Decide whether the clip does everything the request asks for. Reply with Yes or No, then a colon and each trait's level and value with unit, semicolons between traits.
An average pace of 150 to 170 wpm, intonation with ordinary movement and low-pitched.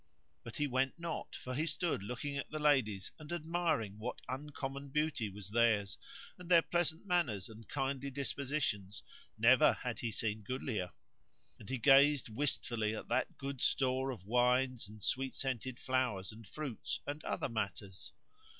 Yes: average, 160 wpm; average, 4.7 semitones; low, 130 Hz